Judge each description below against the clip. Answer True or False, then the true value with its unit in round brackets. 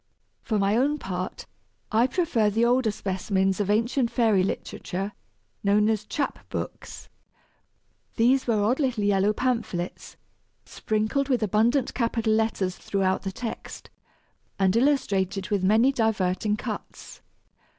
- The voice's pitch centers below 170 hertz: False (215 Hz)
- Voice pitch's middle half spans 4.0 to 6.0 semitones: False (3.5 semitones)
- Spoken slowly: True (125 wpm)